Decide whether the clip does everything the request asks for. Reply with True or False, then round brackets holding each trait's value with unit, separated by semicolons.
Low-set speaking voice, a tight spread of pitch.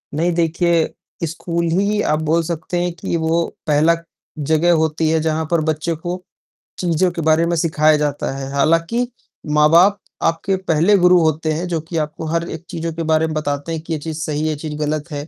False (160 Hz; 1.7 semitones)